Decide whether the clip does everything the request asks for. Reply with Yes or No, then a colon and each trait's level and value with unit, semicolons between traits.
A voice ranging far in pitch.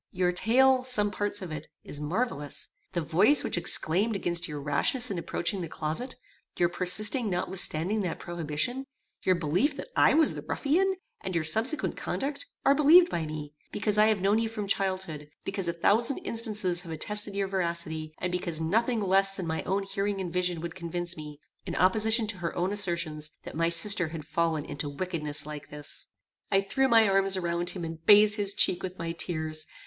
No: average, 4.3 semitones